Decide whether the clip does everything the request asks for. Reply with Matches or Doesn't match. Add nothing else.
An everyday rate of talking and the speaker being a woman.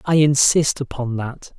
Doesn't match